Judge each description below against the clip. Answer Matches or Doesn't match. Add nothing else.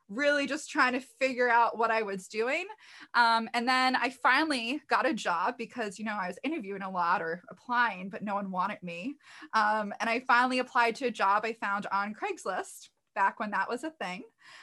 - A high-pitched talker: Matches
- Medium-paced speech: Doesn't match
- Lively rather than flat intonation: Doesn't match